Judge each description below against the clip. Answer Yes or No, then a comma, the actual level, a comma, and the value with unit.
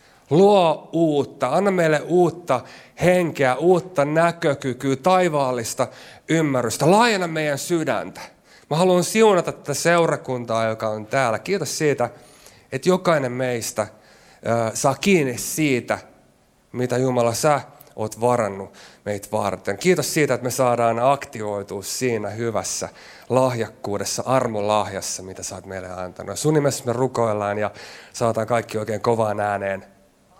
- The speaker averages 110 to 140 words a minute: Yes, average, 120 wpm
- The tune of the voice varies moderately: No, wide, 5.7 semitones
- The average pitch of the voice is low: Yes, low, 125 Hz